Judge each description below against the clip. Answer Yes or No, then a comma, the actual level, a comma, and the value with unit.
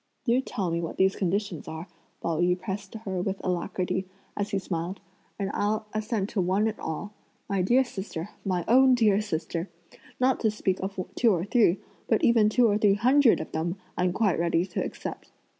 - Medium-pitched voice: No, high, 195 Hz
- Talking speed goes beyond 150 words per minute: Yes, average, 190 wpm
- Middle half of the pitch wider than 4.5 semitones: No, average, 3.3 semitones